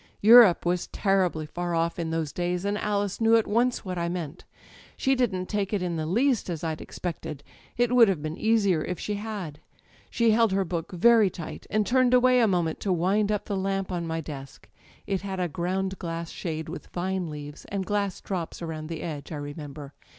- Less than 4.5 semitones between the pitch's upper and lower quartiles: Yes, average, 4.0 semitones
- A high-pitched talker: No, medium, 180 Hz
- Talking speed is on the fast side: Yes, fast, 215 wpm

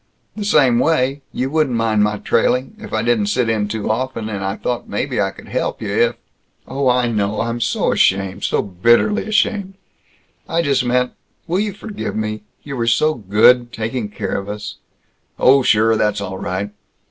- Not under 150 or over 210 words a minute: Yes, average, 195 wpm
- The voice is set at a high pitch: No, low, 120 Hz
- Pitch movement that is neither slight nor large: Yes, average, 4.0 semitones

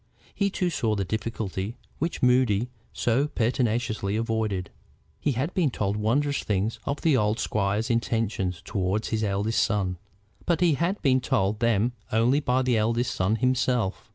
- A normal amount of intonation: Yes, average, 3.7 semitones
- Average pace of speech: Yes, average, 155 wpm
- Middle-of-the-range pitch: No, low, 115 Hz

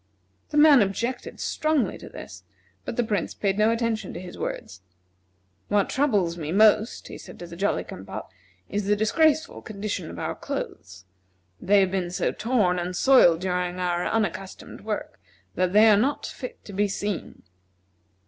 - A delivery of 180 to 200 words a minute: No, average, 170 wpm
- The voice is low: No, high, 205 Hz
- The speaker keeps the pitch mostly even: No, average, 3.9 semitones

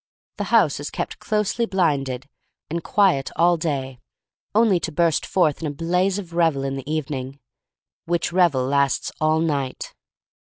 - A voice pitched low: No, medium, 160 Hz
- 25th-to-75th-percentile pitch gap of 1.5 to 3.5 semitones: No, average, 4.3 semitones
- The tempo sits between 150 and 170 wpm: Yes, average, 155 wpm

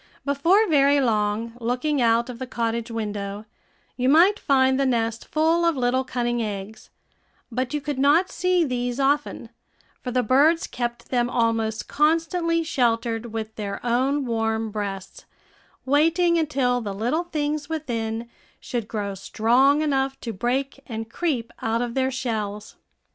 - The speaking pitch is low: No, high, 245 Hz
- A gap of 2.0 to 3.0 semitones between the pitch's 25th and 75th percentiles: No, average, 4.3 semitones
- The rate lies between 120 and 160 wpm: Yes, average, 150 wpm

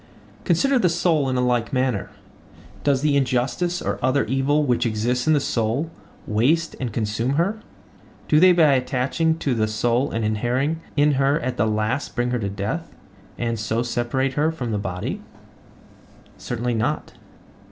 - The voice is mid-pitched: No, low, 130 Hz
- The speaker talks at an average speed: Yes, average, 160 wpm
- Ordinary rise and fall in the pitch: Yes, average, 4.3 semitones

